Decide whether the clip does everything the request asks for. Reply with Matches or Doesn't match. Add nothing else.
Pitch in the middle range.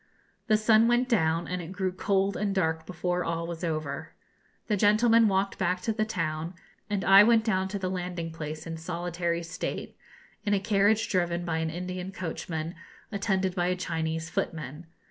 Matches